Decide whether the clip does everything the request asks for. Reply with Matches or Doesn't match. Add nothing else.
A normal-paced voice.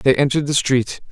Doesn't match